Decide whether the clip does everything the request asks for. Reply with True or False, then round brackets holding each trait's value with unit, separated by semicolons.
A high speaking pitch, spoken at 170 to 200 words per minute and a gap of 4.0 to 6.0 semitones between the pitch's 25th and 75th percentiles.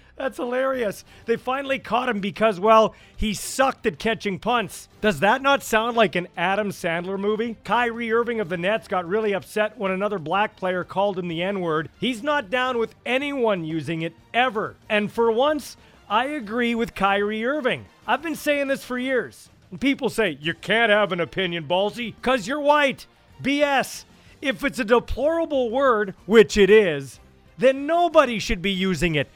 True (220 Hz; 180 wpm; 4.7 semitones)